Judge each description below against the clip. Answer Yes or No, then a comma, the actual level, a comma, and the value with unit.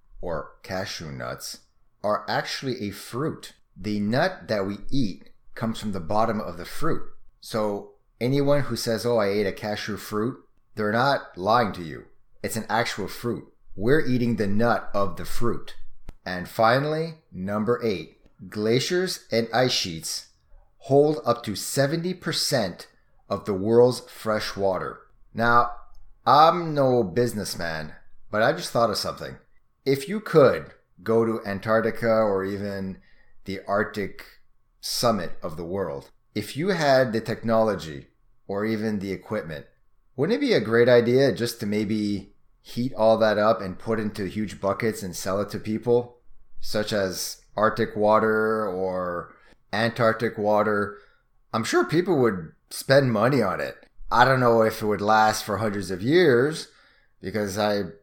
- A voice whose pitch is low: Yes, low, 110 Hz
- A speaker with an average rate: Yes, average, 150 wpm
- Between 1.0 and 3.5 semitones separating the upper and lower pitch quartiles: Yes, average, 2.9 semitones